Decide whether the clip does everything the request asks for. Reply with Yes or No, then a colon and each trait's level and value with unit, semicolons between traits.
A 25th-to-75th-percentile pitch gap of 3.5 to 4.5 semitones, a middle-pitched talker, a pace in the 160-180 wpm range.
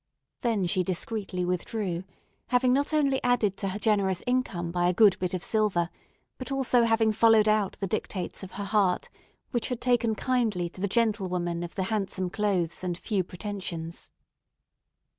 No: average, 4.0 semitones; high, 200 Hz; average, 170 wpm